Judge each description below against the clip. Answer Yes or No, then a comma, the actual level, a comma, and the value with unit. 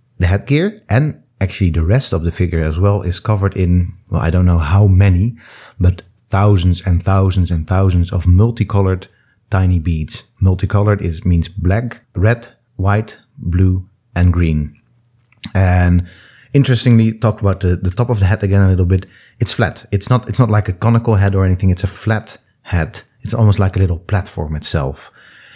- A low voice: Yes, very low, 95 Hz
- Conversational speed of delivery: Yes, average, 180 wpm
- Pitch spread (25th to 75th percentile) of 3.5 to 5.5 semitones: Yes, average, 3.9 semitones